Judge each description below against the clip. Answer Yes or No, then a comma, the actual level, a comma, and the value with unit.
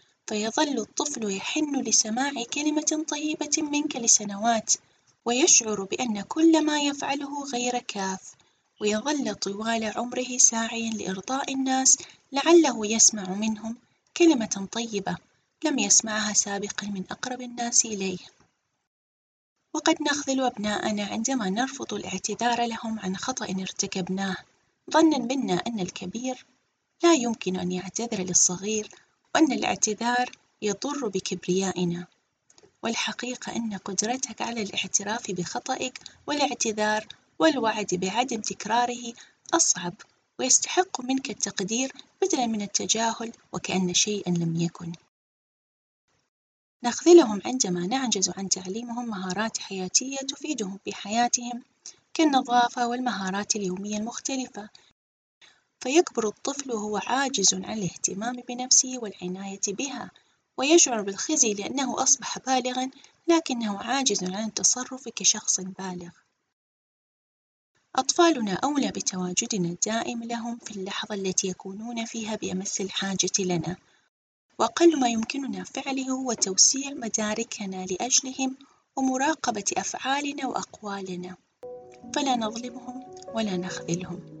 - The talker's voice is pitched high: Yes, high, 225 Hz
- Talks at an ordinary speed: Yes, average, 100 wpm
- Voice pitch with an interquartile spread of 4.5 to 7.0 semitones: Yes, average, 5.2 semitones